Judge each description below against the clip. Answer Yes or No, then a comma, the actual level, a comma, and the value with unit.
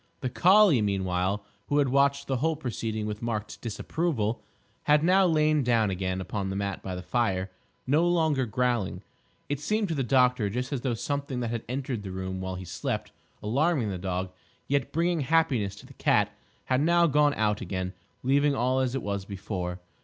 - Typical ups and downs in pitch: No, wide, 6.4 semitones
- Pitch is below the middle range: Yes, low, 125 Hz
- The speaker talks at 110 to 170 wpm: No, average, 190 wpm